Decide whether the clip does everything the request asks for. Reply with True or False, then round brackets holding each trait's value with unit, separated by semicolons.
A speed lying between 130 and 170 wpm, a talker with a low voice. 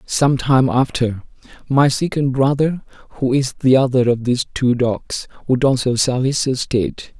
True (160 wpm; 130 Hz)